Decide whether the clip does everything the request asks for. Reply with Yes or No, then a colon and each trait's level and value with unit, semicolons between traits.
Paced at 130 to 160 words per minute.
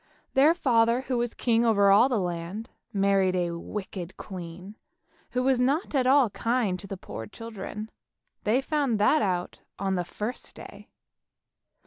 Yes: average, 155 wpm